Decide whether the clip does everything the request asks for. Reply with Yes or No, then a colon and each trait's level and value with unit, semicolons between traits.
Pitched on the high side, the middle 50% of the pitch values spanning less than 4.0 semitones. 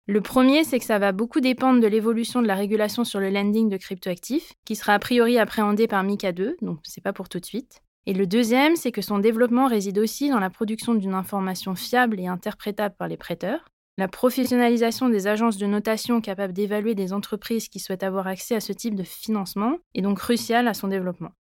Yes: high, 215 Hz; average, 3.2 semitones